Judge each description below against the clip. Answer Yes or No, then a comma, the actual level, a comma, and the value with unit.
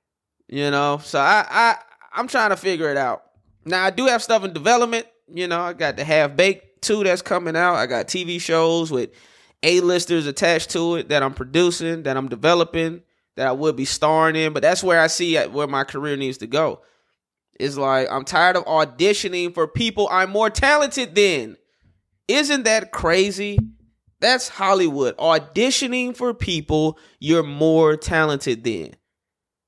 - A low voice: No, medium, 165 Hz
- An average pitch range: Yes, average, 4.8 semitones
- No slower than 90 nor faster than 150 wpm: No, average, 170 wpm